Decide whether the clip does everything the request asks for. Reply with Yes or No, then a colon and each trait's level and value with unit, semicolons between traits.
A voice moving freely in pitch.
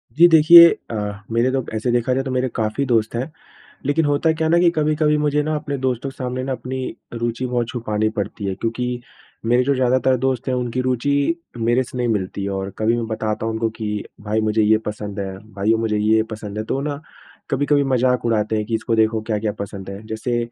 No: average, 3.4 semitones